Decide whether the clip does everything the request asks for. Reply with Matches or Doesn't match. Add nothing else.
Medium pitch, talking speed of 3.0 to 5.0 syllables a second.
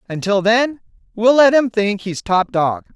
Doesn't match